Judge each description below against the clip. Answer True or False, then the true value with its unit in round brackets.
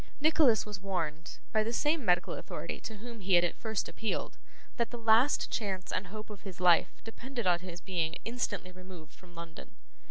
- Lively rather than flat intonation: False (4.3 semitones)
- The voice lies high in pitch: True (195 Hz)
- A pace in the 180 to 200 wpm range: True (190 wpm)